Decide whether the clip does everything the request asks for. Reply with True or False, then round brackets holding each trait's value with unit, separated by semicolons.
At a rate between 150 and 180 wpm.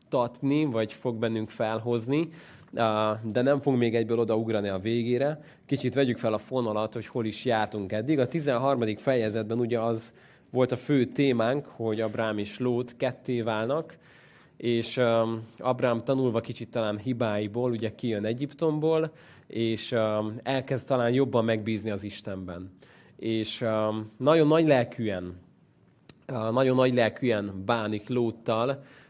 False (130 wpm)